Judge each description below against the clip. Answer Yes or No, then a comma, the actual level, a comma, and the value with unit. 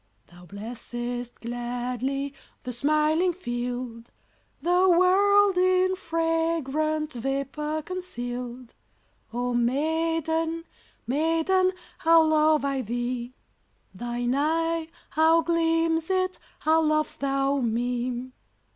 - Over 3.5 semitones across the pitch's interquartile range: Yes, average, 5.1 semitones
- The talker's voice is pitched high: Yes, very high, 300 Hz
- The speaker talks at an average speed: No, slow, 90 wpm